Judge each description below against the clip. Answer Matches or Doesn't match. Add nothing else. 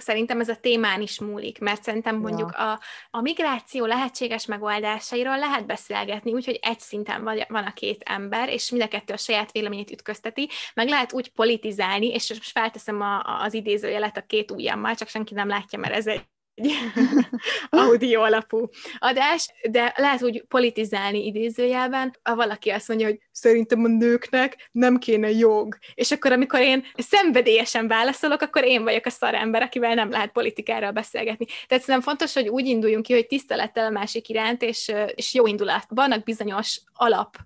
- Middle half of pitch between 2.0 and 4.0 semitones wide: Matches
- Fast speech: Matches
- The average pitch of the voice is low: Doesn't match